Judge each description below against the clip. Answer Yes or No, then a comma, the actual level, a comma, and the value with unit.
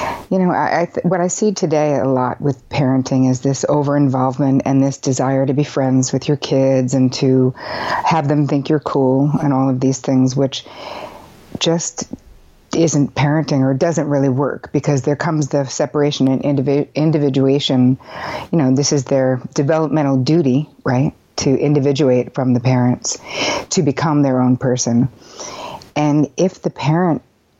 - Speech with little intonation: Yes, narrow, 2.2 semitones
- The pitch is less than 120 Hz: No, medium, 140 Hz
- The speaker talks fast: No, average, 165 wpm